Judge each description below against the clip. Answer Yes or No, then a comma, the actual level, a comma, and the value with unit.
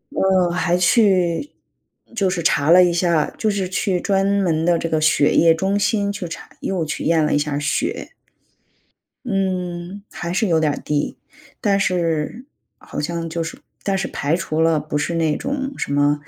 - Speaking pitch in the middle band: Yes, medium, 175 Hz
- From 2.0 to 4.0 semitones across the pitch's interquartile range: Yes, average, 3.3 semitones